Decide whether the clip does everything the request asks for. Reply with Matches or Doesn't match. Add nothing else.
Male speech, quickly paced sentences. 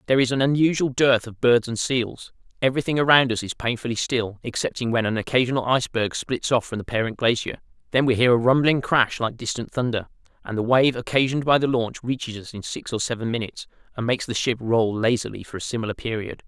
Matches